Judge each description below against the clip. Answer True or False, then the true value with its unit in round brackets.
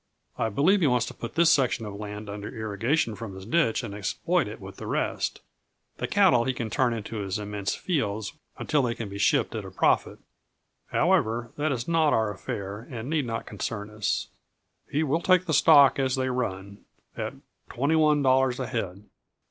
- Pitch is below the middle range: True (115 Hz)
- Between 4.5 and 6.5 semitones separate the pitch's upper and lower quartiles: True (5.2 semitones)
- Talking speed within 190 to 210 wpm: True (195 wpm)